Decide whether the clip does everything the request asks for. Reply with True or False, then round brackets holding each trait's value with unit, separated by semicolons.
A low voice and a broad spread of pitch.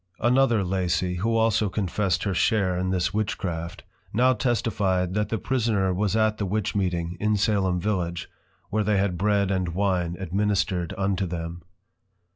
False (95 Hz; 2.9 semitones)